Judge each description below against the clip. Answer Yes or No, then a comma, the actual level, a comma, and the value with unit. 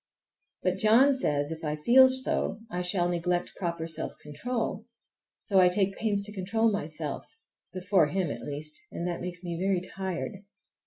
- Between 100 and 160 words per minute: Yes, average, 155 wpm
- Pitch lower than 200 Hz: Yes, medium, 185 Hz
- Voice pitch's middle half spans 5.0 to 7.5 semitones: No, average, 3.6 semitones